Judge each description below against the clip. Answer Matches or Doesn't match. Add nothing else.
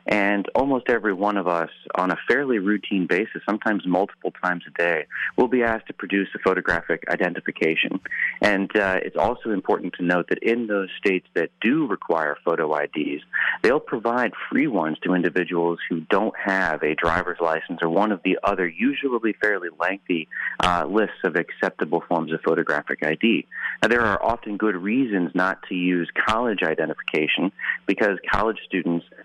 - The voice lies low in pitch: Matches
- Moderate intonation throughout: Matches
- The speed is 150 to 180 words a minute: Matches